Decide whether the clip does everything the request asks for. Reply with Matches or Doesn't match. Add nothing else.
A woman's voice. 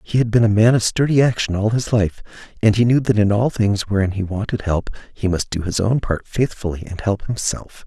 Doesn't match